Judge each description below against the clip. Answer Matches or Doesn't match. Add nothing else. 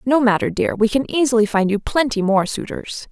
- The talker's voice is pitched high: Matches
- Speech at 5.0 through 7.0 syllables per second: Matches